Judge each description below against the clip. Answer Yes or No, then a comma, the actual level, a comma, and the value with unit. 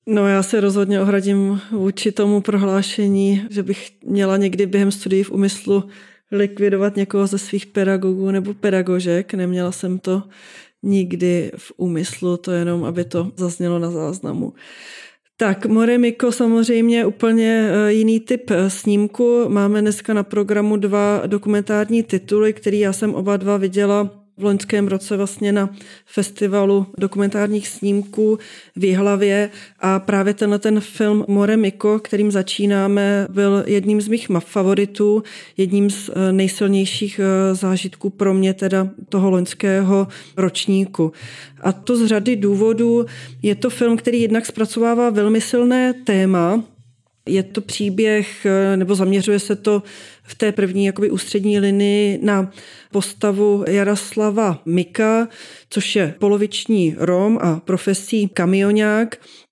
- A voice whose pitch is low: No, high, 200 Hz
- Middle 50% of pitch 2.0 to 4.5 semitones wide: No, narrow, 1.6 semitones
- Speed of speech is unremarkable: Yes, average, 130 wpm